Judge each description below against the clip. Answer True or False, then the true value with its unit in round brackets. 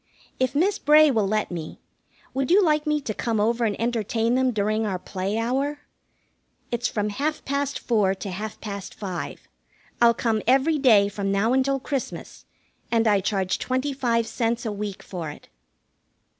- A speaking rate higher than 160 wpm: True (170 wpm)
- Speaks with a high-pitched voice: True (230 Hz)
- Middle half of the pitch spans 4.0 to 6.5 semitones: True (4.5 semitones)